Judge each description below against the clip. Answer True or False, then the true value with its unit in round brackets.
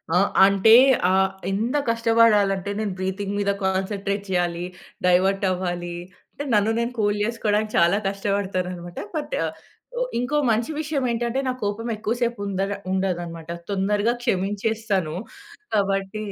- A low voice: False (200 Hz)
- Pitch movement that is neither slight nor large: True (3.0 semitones)